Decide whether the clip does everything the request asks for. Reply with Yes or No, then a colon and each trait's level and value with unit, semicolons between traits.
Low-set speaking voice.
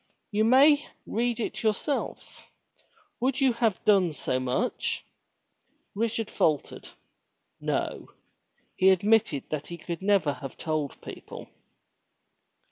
No: high, 205 Hz